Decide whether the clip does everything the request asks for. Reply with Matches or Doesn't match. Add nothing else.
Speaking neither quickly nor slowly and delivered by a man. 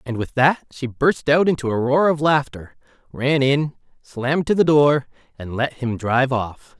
Matches